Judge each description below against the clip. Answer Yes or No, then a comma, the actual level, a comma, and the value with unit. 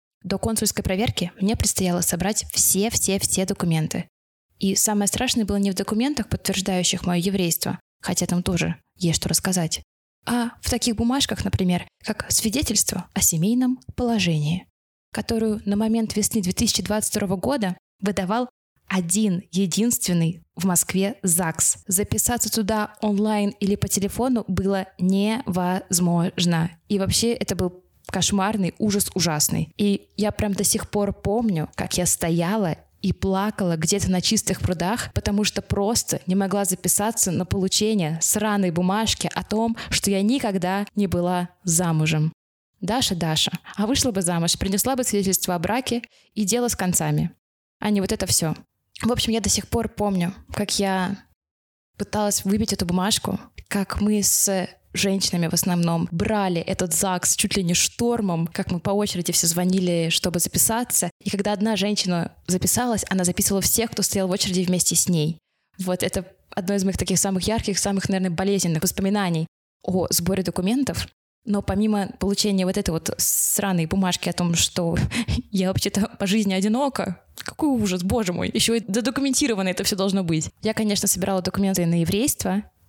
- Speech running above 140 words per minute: Yes, average, 155 wpm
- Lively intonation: No, average, 2.8 semitones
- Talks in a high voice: Yes, high, 195 Hz